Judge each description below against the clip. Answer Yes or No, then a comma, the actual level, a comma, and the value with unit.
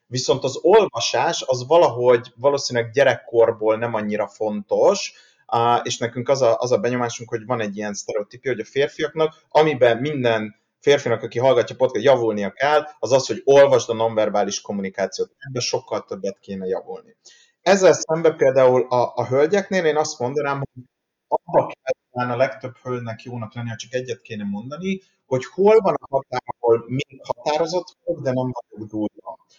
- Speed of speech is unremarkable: No, fast, 160 wpm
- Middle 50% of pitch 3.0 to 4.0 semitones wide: No, average, 4.4 semitones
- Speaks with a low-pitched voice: Yes, low, 125 Hz